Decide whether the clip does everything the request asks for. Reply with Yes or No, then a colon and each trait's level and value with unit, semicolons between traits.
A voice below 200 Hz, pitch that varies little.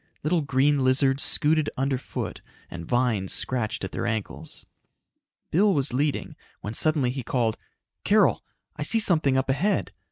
No: low, 135 Hz; average, 3.5 semitones